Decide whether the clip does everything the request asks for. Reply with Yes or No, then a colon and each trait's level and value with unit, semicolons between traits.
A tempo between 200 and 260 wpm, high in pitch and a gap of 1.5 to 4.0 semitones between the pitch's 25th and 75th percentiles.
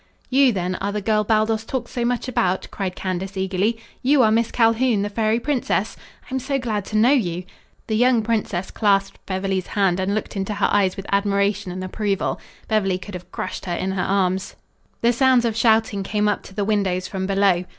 Yes: fast, 205 wpm; high, 205 Hz; average, 3.0 semitones